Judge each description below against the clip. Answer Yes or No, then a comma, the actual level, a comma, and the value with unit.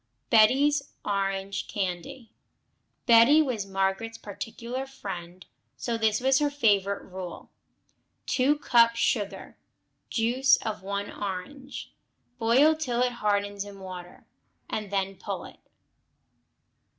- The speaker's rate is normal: No, slow, 110 wpm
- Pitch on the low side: No, high, 220 Hz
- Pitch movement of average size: Yes, average, 4.6 semitones